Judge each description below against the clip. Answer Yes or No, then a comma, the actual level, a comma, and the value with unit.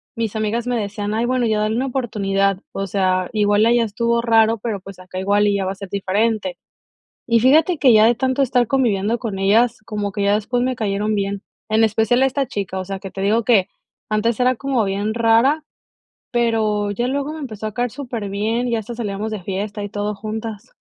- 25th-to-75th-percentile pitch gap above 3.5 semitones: No, average, 2.9 semitones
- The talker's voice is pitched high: Yes, high, 220 Hz